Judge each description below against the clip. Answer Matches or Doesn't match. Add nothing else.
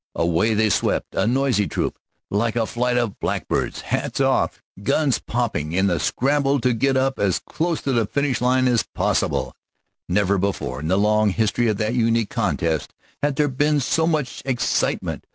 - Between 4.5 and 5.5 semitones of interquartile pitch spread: Matches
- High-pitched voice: Doesn't match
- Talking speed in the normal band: Matches